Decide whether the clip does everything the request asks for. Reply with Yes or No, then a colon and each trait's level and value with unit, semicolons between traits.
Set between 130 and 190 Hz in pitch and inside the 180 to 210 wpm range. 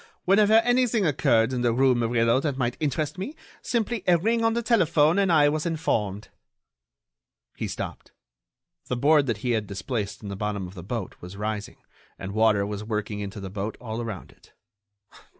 No: low, 120 Hz; average, 185 wpm